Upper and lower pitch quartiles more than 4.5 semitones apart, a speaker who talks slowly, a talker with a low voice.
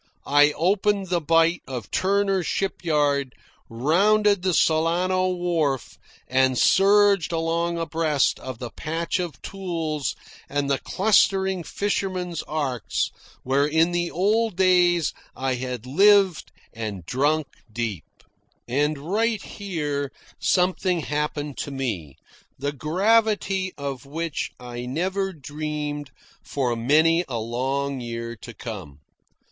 No: wide, 5.5 semitones; slow, 115 wpm; medium, 155 Hz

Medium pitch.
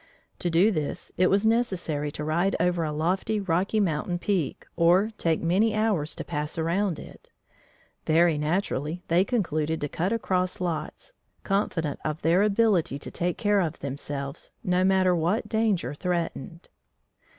Yes: medium, 175 Hz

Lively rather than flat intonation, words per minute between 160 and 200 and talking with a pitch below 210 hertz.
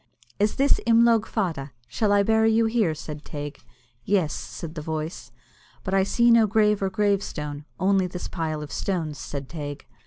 Yes: wide, 5.8 semitones; average, 175 wpm; high, 190 Hz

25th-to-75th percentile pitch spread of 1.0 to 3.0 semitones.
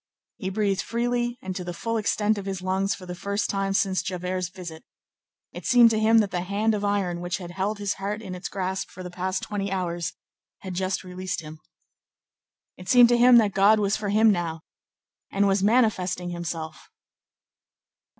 Yes: narrow, 2.5 semitones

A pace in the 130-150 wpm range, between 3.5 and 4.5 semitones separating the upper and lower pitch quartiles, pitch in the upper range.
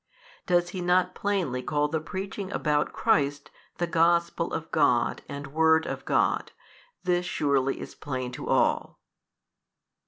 No: slow, 135 wpm; average, 3.8 semitones; medium, 160 Hz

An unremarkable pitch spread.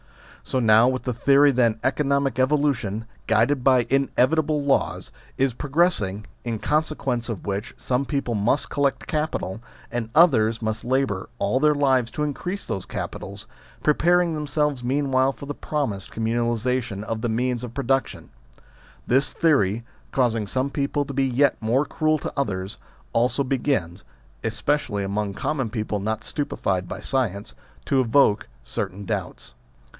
Yes: average, 4.3 semitones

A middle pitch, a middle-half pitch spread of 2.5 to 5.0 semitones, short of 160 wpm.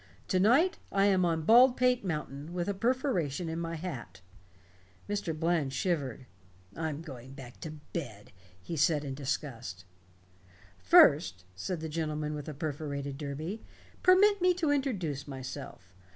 No: medium, 155 Hz; wide, 5.6 semitones; average, 145 wpm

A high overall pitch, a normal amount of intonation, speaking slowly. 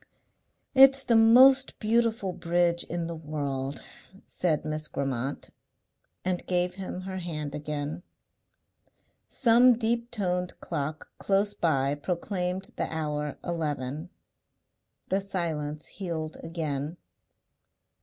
No: medium, 170 Hz; average, 4.6 semitones; slow, 105 wpm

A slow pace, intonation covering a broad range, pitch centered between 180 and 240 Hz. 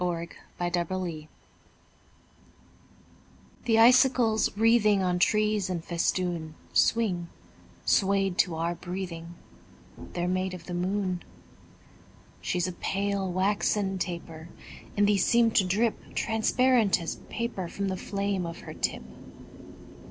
No: slow, 115 wpm; average, 3.1 semitones; high, 190 Hz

